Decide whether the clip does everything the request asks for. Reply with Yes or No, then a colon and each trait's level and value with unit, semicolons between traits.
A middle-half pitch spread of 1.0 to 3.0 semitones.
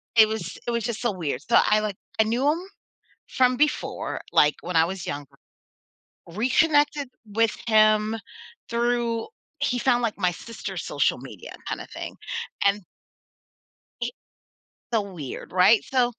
No: average, 3.8 semitones